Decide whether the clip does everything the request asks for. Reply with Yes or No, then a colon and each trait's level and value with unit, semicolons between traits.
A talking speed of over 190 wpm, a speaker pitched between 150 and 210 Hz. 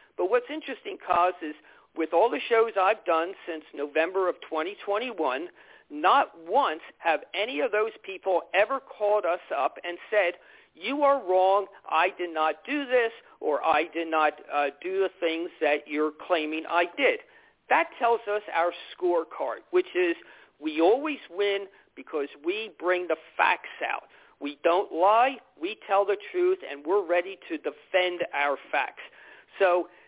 No: average, 160 wpm; high, 190 Hz